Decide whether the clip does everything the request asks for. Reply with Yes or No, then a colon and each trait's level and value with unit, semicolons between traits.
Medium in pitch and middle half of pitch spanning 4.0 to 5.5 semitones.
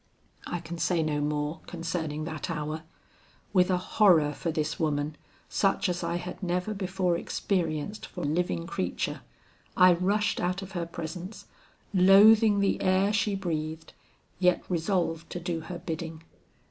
No: medium, 175 Hz; average, 2.9 semitones